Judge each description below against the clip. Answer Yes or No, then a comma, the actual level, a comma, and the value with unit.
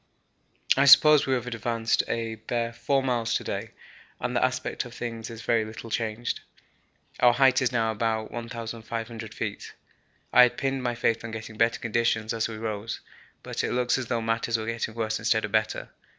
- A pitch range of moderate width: No, narrow, 1.4 semitones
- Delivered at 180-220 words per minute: Yes, average, 190 wpm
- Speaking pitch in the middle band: No, low, 115 Hz